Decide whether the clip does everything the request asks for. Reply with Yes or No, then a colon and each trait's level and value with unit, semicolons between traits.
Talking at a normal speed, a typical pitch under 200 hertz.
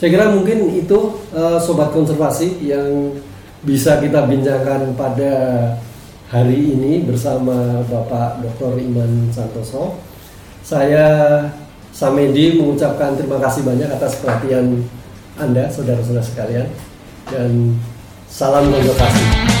Yes: average, 100 wpm; low, 135 Hz